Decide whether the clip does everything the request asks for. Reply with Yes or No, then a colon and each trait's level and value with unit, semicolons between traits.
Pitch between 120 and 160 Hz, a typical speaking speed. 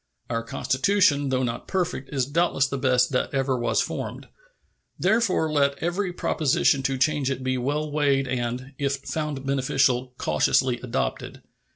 Yes: low, 135 Hz; average, 150 wpm